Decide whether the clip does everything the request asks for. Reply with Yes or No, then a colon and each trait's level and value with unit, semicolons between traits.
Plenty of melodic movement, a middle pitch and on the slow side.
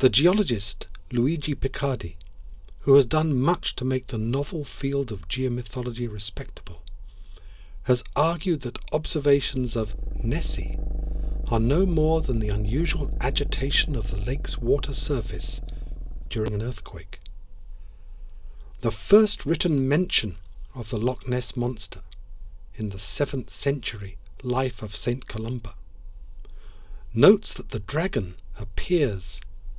No: wide, 6.2 semitones; low, 110 Hz; slow, 120 wpm